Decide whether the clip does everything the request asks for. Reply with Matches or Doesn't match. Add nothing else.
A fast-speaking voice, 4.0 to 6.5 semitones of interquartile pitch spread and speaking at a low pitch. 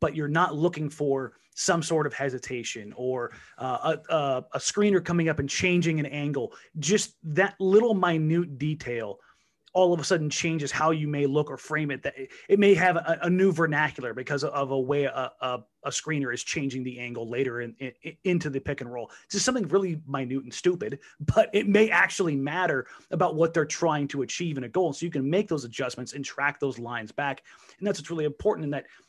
Doesn't match